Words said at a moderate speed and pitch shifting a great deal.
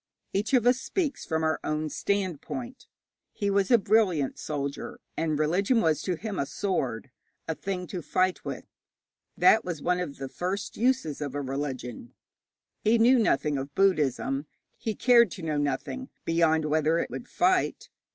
Yes: average, 170 wpm; wide, 6.5 semitones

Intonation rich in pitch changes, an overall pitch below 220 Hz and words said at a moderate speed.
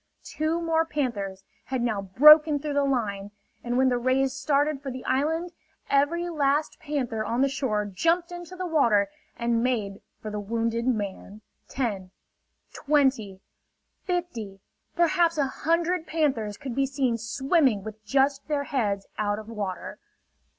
No: wide, 5.8 semitones; very high, 265 Hz; average, 150 wpm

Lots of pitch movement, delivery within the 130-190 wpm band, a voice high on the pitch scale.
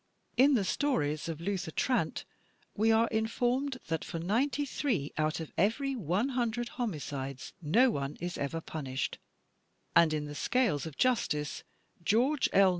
Yes: wide, 8.2 semitones; average, 150 wpm; high, 200 Hz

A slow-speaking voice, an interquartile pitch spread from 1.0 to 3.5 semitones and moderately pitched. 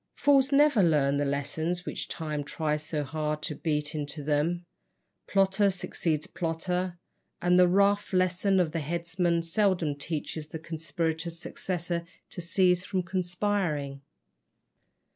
Yes: slow, 130 wpm; average, 3.2 semitones; medium, 170 Hz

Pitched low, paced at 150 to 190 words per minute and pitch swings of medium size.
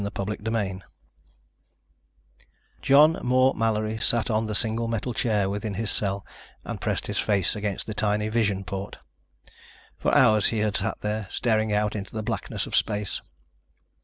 No: low, 110 Hz; average, 155 wpm; narrow, 1.6 semitones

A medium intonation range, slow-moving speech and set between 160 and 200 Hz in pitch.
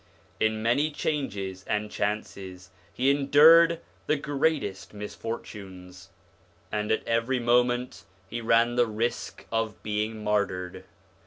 No: average, 3.6 semitones; slow, 110 wpm; low, 115 Hz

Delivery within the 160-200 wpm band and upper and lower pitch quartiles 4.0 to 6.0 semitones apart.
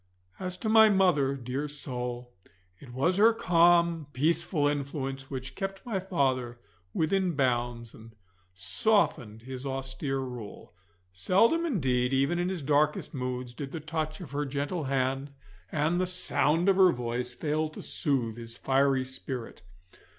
No: average, 145 wpm; average, 5.2 semitones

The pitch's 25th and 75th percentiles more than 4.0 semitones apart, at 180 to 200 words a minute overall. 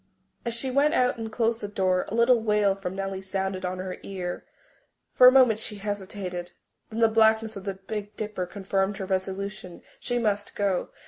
No: average, 2.7 semitones; average, 190 wpm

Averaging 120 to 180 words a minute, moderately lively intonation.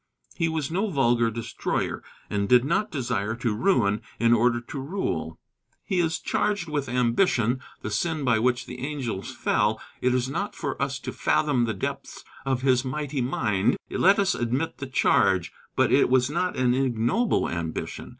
Yes: average, 170 wpm; average, 4.3 semitones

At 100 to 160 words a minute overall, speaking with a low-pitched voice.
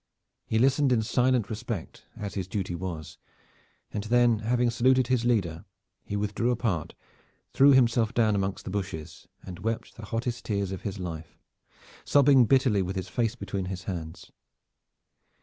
Yes: average, 155 wpm; low, 110 Hz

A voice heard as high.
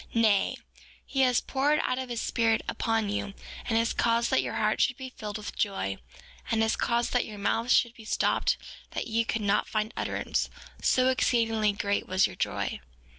Yes: high, 225 Hz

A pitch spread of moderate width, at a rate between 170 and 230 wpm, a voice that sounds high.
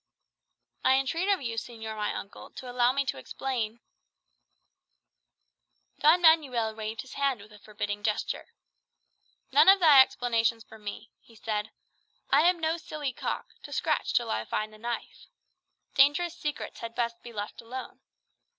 No: average, 4.4 semitones; average, 160 wpm; high, 240 Hz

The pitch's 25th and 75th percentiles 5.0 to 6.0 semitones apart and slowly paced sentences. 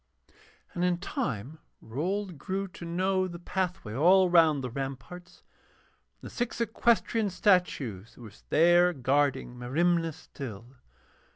Yes: wide, 5.6 semitones; slow, 125 wpm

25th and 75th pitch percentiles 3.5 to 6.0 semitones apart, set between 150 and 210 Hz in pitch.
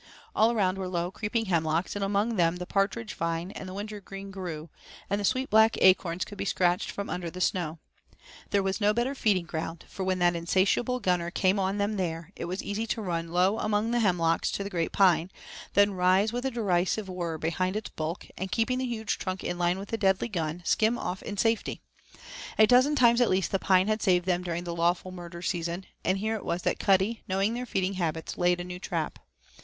No: average, 3.1 semitones; high, 190 Hz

